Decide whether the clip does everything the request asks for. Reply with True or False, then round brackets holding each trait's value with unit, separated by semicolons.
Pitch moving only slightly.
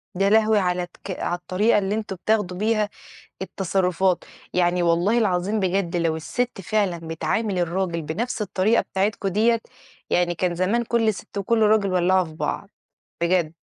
False (3.2 semitones)